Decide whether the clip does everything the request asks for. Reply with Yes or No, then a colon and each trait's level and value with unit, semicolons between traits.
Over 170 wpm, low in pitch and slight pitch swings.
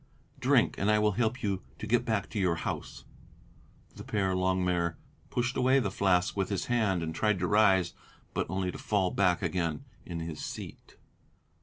No: average, 180 wpm; very low, 95 Hz; average, 3.1 semitones